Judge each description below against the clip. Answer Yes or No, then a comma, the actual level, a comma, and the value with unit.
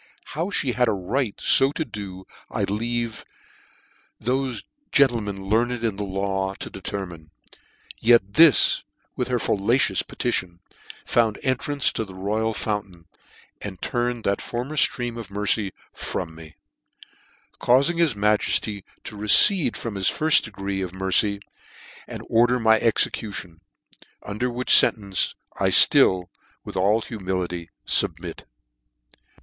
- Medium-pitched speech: No, low, 105 Hz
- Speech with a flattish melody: No, average, 3.9 semitones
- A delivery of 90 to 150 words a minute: Yes, slow, 135 wpm